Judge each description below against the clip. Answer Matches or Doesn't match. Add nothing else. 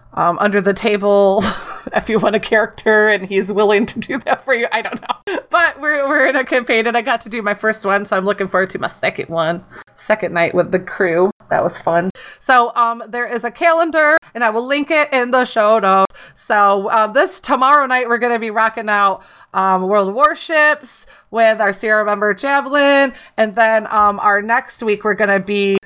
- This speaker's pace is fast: Matches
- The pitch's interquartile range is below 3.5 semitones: Doesn't match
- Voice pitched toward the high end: Matches